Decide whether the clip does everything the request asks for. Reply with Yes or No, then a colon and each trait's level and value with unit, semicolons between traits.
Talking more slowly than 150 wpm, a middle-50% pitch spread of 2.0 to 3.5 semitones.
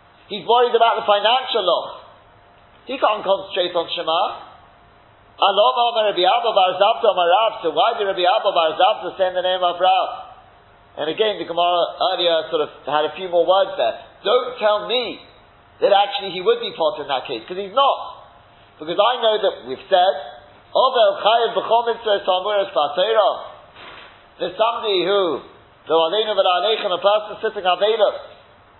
No: average, 140 wpm; average, 4.2 semitones